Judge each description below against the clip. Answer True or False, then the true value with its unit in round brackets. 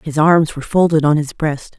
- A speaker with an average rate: False (235 wpm)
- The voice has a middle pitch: True (155 Hz)